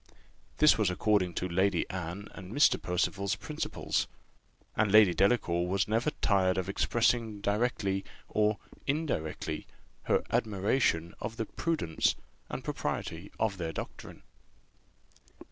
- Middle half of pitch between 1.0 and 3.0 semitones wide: No, average, 3.4 semitones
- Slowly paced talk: Yes, slow, 120 wpm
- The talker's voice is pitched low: Yes, low, 100 Hz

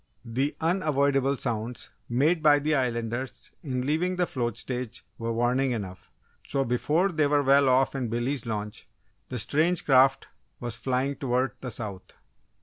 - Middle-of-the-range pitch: No, low, 130 Hz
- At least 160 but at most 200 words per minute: No, average, 150 wpm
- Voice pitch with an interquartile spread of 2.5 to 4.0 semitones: Yes, average, 3.3 semitones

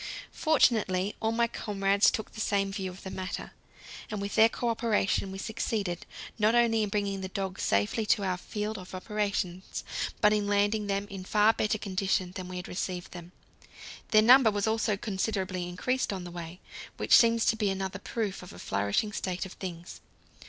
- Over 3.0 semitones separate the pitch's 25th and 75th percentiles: No, narrow, 2.6 semitones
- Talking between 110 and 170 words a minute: No, average, 185 wpm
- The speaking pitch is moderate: No, high, 200 Hz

